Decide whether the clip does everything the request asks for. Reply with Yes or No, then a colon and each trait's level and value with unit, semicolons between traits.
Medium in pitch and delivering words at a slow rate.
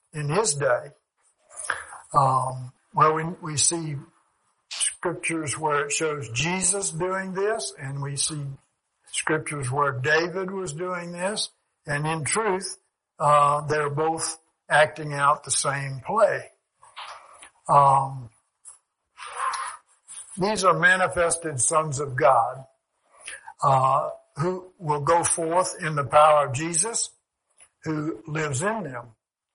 Yes: medium, 155 Hz; slow, 110 wpm